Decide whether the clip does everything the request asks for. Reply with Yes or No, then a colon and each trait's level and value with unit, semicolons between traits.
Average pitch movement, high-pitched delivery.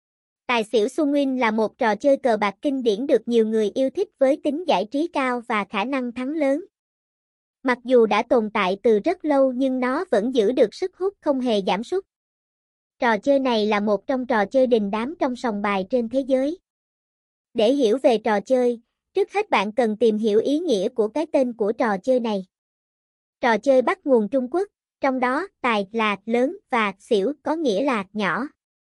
Yes: average, 4.5 semitones; very high, 255 Hz